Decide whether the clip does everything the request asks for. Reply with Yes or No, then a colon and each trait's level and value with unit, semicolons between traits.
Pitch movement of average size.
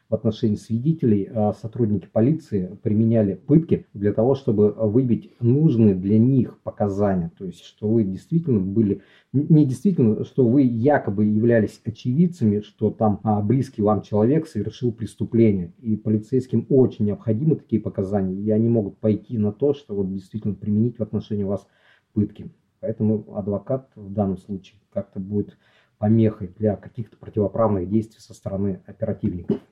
No: narrow, 2.2 semitones